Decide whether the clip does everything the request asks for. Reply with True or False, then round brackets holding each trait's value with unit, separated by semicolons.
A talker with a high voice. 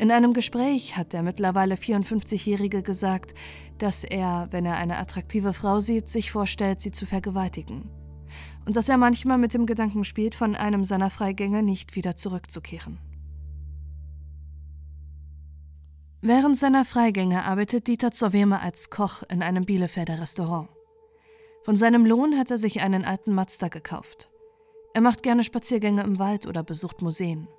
True (195 Hz)